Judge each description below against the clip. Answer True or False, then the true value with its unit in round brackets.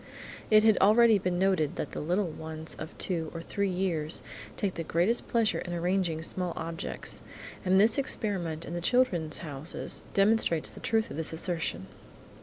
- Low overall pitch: False (180 Hz)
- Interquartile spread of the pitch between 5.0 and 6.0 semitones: False (3.9 semitones)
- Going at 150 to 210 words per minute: True (165 wpm)